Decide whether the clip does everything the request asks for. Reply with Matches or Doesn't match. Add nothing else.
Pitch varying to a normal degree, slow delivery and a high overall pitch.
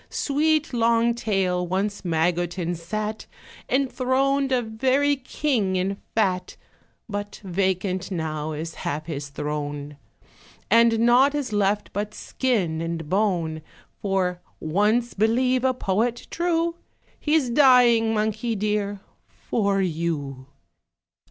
Doesn't match